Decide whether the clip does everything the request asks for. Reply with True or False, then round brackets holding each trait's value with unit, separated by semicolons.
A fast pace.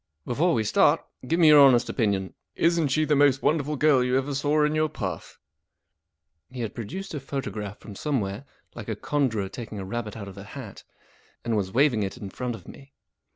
True (210 wpm)